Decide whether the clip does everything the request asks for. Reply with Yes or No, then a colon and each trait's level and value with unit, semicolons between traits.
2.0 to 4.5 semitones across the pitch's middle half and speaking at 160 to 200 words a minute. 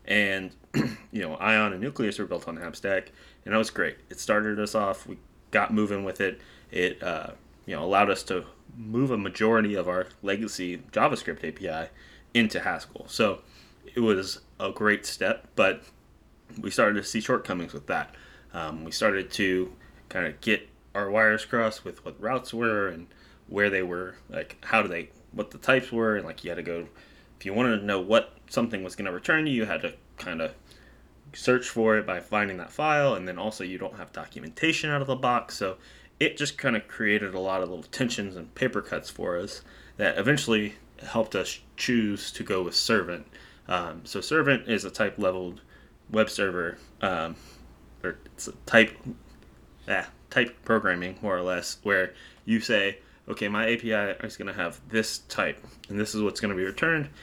Yes: average, 3.5 semitones; average, 195 wpm